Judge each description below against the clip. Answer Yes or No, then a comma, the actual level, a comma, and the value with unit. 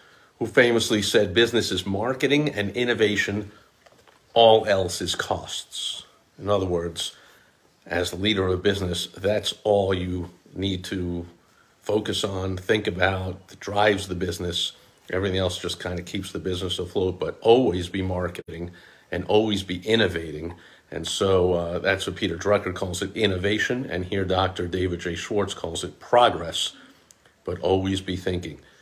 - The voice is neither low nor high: No, very low, 95 Hz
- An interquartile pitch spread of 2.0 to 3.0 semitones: Yes, narrow, 2.5 semitones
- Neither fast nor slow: Yes, average, 155 wpm